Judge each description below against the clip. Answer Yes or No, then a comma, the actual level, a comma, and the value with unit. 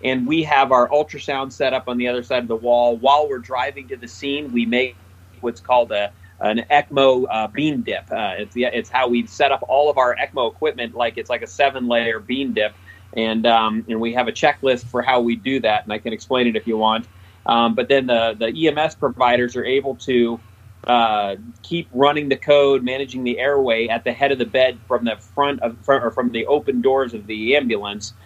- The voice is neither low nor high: No, low, 120 Hz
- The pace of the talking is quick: Yes, fast, 230 wpm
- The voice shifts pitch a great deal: No, average, 3.3 semitones